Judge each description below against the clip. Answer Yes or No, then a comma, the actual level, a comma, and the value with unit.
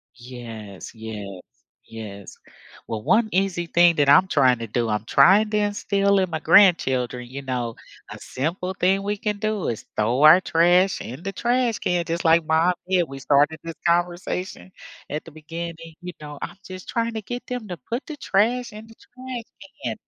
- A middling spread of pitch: No, wide, 6.9 semitones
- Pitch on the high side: No, medium, 170 Hz